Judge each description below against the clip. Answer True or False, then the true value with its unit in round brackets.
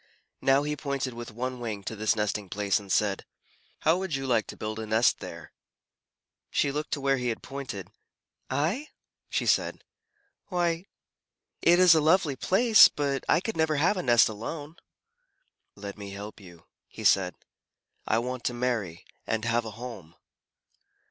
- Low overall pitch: True (125 Hz)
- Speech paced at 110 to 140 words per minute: False (165 wpm)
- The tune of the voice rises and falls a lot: True (5.8 semitones)